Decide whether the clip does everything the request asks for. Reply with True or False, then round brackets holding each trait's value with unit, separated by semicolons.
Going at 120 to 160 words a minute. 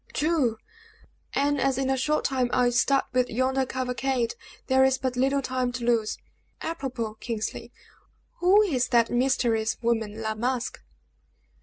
True (145 wpm)